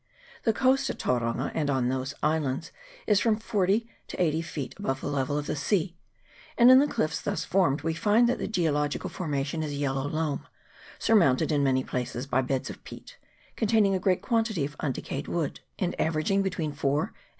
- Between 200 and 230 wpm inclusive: Yes, fast, 205 wpm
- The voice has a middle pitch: Yes, medium, 155 Hz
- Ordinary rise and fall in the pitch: No, wide, 5.9 semitones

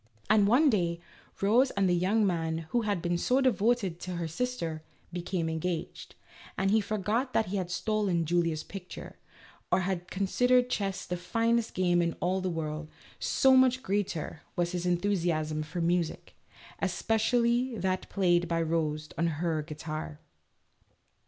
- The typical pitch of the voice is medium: Yes, medium, 180 Hz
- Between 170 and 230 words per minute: No, average, 155 wpm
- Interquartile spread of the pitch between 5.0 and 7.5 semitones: No, average, 4.3 semitones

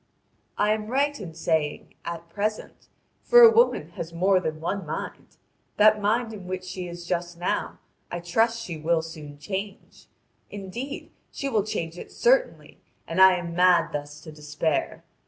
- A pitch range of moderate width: Yes, average, 4.4 semitones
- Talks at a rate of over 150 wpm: Yes, average, 165 wpm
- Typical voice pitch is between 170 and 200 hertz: Yes, medium, 185 Hz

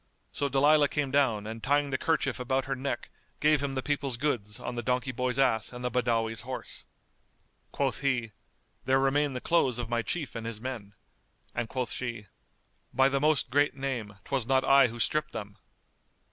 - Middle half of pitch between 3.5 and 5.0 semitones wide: No, average, 2.9 semitones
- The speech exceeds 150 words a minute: Yes, average, 190 wpm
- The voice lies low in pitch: Yes, low, 130 Hz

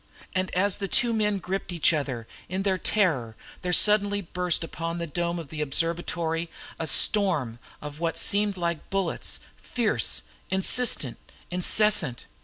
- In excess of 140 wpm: Yes, average, 150 wpm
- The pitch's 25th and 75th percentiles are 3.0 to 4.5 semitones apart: Yes, average, 3.5 semitones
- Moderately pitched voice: Yes, medium, 175 Hz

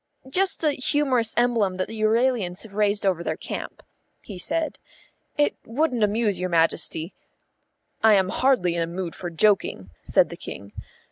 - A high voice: Yes, high, 210 Hz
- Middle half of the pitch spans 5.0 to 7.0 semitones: Yes, wide, 5.4 semitones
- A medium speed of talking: Yes, average, 160 wpm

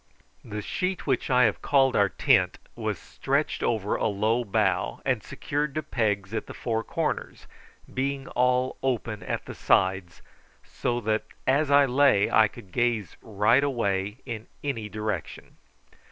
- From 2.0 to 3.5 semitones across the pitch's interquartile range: No, average, 4.2 semitones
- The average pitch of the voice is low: Yes, low, 115 Hz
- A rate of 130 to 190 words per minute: Yes, average, 155 wpm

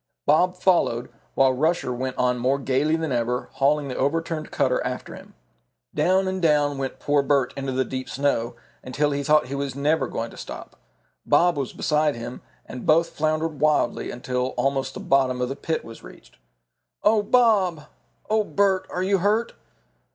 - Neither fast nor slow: Yes, average, 180 wpm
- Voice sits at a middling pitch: Yes, medium, 145 Hz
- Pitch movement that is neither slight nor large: Yes, average, 4.1 semitones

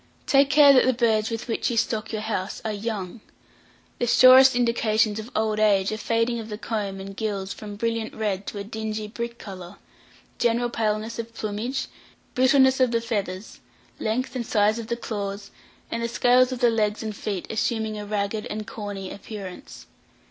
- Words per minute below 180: No, average, 185 wpm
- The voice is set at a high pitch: Yes, high, 220 Hz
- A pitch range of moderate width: No, narrow, 2.2 semitones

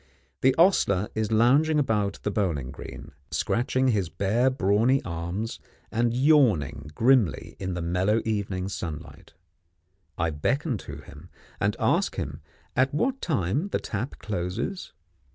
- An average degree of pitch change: No, wide, 6.3 semitones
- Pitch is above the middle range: No, low, 105 Hz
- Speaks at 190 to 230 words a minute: No, slow, 135 wpm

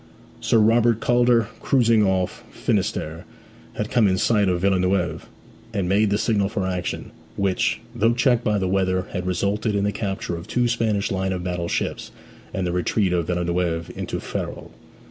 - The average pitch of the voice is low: Yes, low, 100 Hz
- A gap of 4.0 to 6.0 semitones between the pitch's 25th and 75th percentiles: No, average, 3.3 semitones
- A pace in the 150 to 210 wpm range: Yes, average, 170 wpm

